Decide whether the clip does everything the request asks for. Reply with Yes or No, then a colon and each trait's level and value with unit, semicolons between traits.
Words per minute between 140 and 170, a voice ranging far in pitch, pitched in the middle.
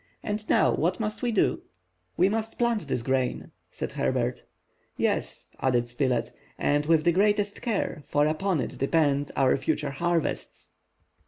Yes: average, 150 wpm; wide, 7.0 semitones; medium, 160 Hz